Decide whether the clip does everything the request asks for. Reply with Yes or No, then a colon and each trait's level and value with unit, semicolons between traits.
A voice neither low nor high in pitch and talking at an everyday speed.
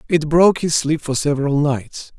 Yes: medium, 150 Hz; average, 190 wpm